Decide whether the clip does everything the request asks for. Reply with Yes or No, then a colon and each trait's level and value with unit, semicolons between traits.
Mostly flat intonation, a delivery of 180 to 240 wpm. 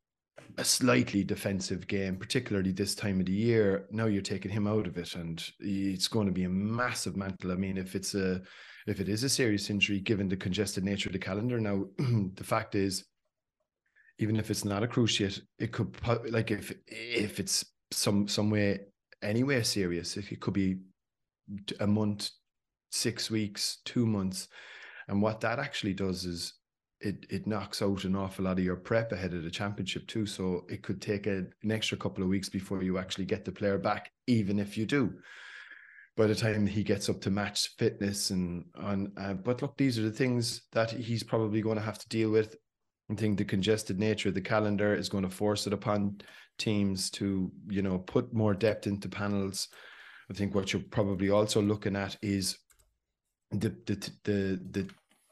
Yes: narrow, 2.0 semitones; average, 195 wpm